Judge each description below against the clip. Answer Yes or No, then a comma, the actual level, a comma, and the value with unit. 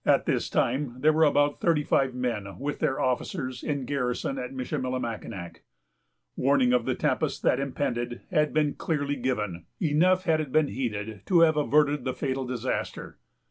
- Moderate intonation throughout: Yes, average, 3.5 semitones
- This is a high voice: No, low, 135 Hz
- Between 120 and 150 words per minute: No, average, 165 wpm